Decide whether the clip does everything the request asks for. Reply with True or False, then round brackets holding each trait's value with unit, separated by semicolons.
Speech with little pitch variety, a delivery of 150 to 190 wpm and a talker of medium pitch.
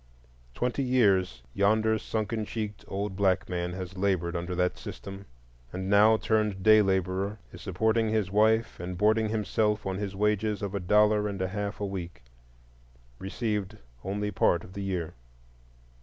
False (2.3 semitones; 155 wpm; 100 Hz)